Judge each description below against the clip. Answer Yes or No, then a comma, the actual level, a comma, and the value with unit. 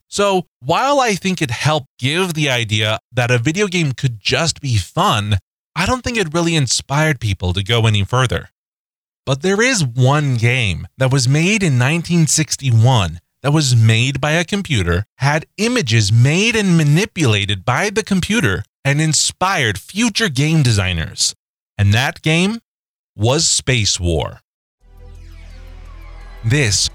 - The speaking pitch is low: Yes, low, 130 Hz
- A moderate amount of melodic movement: No, wide, 7.6 semitones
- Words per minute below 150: Yes, average, 140 wpm